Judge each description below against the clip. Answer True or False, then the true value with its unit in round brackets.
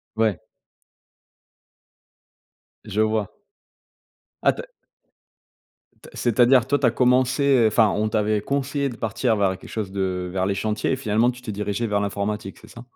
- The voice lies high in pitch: False (110 Hz)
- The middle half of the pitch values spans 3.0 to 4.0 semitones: True (3.4 semitones)